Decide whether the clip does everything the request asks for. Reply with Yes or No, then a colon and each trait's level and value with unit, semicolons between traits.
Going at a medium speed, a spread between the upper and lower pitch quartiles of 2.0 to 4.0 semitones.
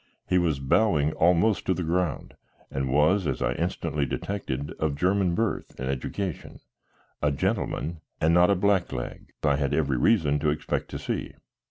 No: average, 165 wpm; average, 4.5 semitones